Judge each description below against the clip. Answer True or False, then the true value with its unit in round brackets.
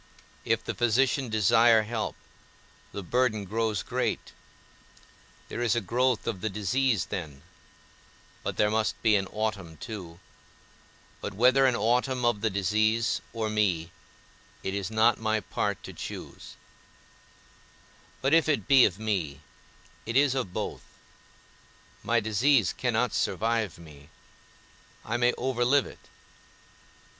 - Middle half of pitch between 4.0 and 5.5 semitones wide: False (3.3 semitones)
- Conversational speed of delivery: False (130 wpm)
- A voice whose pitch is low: True (110 Hz)